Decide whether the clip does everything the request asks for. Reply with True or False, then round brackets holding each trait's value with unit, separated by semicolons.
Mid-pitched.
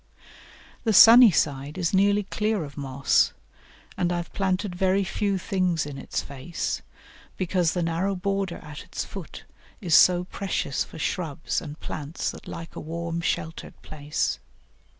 True (175 Hz)